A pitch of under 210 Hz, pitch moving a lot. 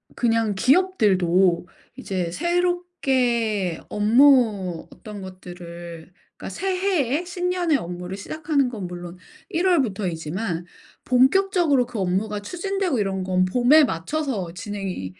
No: high, 220 Hz; wide, 8.9 semitones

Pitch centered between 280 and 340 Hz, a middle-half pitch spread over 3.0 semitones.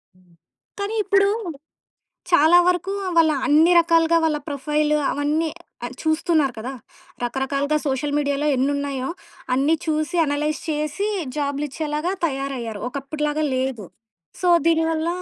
No: very high, 300 Hz; average, 2.7 semitones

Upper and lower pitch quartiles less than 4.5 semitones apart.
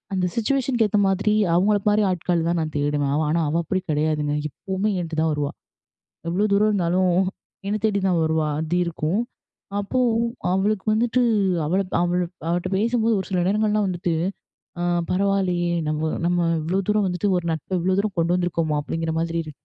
Yes: average, 4.0 semitones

